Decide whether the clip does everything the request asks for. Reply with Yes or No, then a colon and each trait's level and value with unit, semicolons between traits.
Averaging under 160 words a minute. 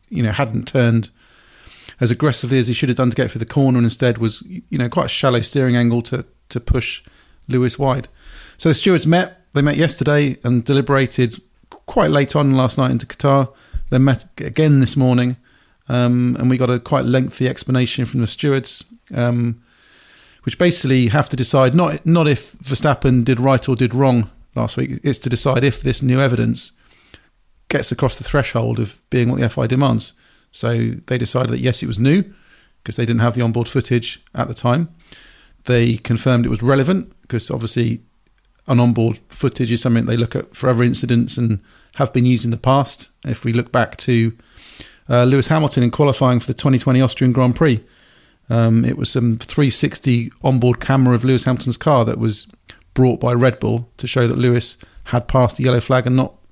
No: average, 195 wpm